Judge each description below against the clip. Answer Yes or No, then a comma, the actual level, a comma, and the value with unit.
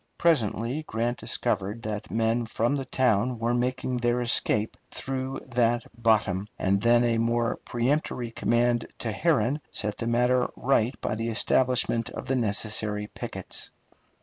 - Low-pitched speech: Yes, low, 120 Hz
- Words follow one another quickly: No, average, 145 wpm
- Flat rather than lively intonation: Yes, narrow, 2.0 semitones